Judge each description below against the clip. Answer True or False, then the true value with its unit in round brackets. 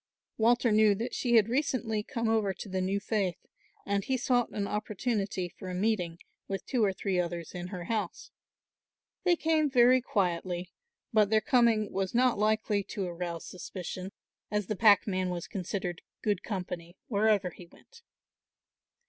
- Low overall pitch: False (205 Hz)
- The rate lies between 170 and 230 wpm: False (160 wpm)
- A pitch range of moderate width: True (3.7 semitones)